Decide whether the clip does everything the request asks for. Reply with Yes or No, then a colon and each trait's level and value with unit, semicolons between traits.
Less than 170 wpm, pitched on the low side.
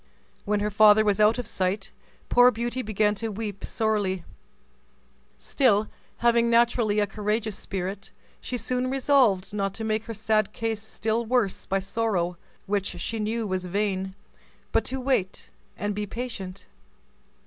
No: average, 150 wpm; high, 215 Hz